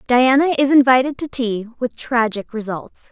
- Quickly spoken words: No, average, 155 wpm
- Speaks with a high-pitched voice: Yes, very high, 250 Hz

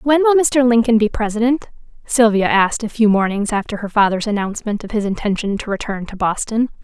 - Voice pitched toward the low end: No, high, 220 Hz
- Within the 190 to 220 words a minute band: Yes, average, 195 wpm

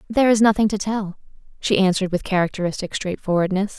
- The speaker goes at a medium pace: Yes, average, 160 wpm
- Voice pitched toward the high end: Yes, high, 195 Hz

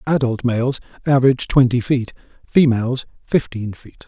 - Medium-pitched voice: No, low, 125 Hz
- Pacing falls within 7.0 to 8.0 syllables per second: No, 5.1 syllables/s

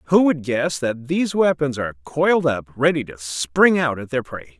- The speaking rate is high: Yes, fast, 210 wpm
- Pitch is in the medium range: Yes, medium, 145 Hz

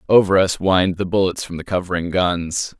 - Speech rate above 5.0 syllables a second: Yes, 5.4 syllables/s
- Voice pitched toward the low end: Yes, very low, 90 Hz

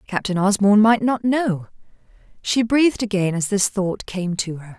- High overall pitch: Yes, high, 205 Hz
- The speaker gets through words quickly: No, average, 175 wpm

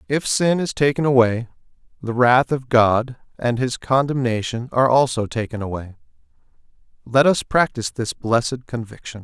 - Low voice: Yes, low, 125 Hz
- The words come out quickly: No, average, 145 wpm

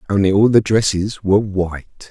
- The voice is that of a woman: No, male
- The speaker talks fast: No, average, 170 wpm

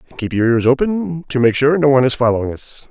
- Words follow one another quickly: Yes, fast, 270 wpm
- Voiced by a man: Yes, male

